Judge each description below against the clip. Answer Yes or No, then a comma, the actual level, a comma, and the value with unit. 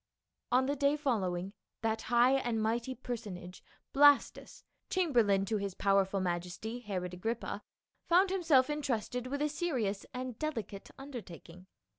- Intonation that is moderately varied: No, wide, 5.8 semitones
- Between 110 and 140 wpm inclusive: Yes, slow, 135 wpm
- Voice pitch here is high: Yes, high, 235 Hz